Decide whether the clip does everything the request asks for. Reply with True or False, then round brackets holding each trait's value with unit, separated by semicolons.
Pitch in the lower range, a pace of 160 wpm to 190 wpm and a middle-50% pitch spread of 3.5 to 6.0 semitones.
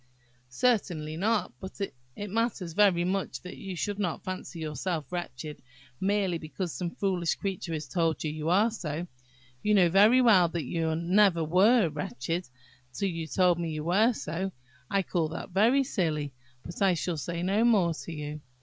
False (175 Hz; 175 wpm; 3.8 semitones)